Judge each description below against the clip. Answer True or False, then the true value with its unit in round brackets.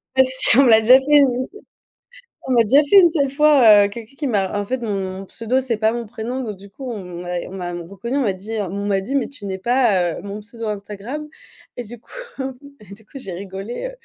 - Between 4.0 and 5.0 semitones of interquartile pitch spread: True (4.7 semitones)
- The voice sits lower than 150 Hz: False (225 Hz)